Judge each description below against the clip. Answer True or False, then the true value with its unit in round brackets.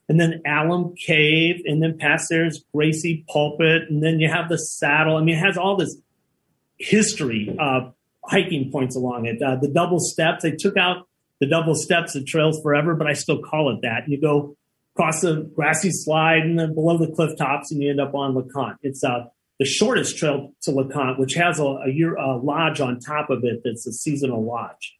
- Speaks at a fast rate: True (210 wpm)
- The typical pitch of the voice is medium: True (155 Hz)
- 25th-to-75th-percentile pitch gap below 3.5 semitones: True (3.0 semitones)